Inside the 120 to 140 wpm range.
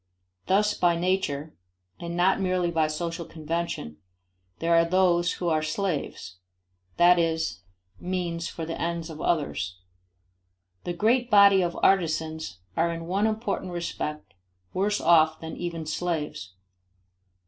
Yes: slow, 135 wpm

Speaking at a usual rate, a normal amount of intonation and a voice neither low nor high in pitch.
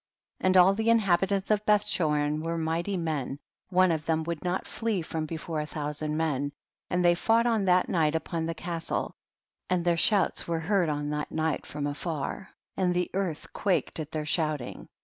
Yes: average, 195 wpm; average, 3.3 semitones; medium, 165 Hz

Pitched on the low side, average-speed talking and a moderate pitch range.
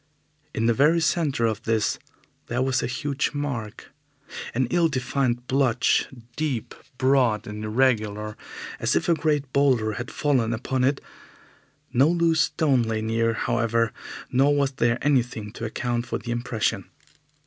Yes: low, 125 Hz; average, 150 wpm; average, 3.6 semitones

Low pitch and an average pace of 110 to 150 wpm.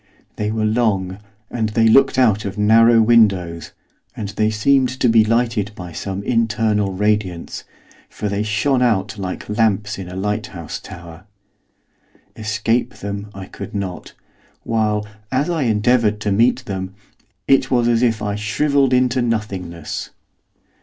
Yes: low, 105 Hz; average, 145 wpm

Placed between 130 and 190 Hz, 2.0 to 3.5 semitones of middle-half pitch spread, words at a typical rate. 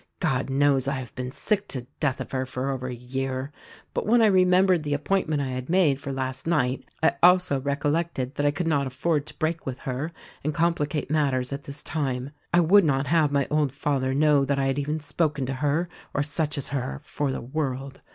No: medium, 140 Hz; average, 2.9 semitones; fast, 220 wpm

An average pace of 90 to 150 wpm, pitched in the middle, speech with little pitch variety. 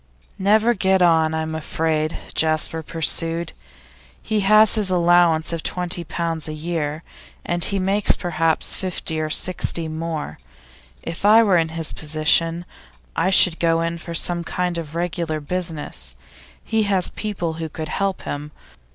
Yes: average, 145 wpm; medium, 165 Hz; narrow, 2.3 semitones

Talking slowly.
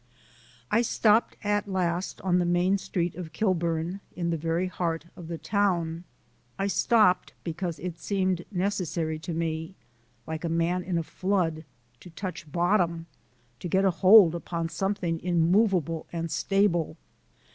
No: average, 145 wpm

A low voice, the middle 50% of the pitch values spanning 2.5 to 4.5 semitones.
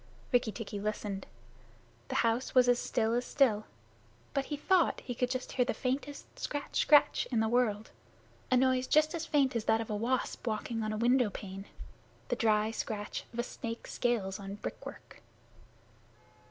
No: high, 240 Hz; average, 3.1 semitones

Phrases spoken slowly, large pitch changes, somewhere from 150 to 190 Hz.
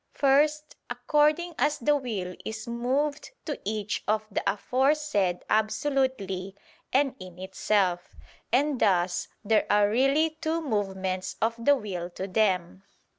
No: slow, 125 wpm; wide, 6.9 semitones; high, 220 Hz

